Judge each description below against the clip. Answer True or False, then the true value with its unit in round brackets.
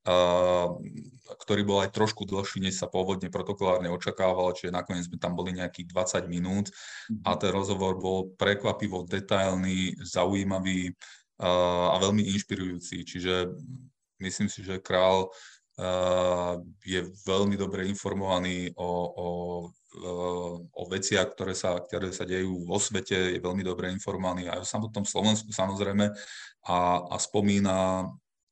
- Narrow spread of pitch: True (1.7 semitones)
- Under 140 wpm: True (125 wpm)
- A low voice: True (95 Hz)